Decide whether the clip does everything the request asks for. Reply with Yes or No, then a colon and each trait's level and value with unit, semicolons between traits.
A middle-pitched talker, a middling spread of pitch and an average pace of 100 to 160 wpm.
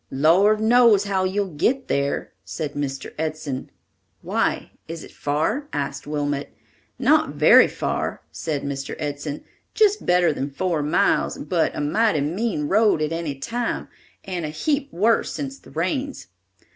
No: medium, 165 Hz; wide, 6.8 semitones; average, 145 wpm